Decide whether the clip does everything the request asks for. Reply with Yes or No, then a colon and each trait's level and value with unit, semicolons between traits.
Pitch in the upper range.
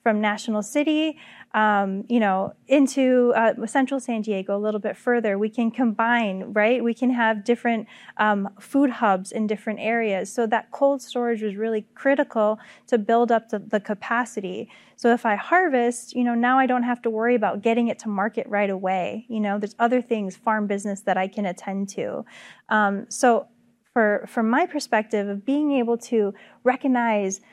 Yes: high, 225 Hz